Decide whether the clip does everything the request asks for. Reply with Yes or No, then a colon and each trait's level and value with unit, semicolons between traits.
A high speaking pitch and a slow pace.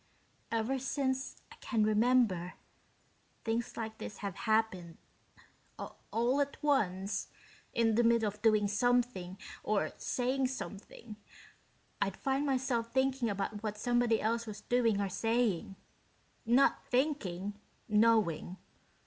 Yes: high, 225 Hz; slow, 115 wpm